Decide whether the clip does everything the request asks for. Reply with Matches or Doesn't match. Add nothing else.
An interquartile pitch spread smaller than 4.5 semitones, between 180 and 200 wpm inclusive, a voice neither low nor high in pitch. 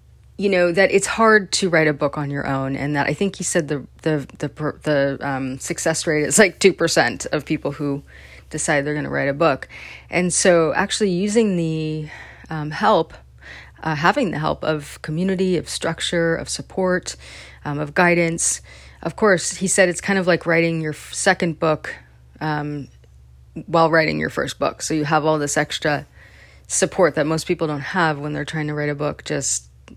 Matches